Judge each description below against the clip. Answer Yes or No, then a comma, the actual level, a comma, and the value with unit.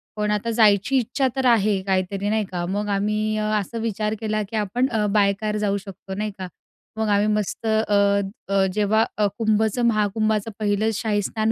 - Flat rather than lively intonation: Yes, narrow, 1.4 semitones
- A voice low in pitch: No, high, 210 Hz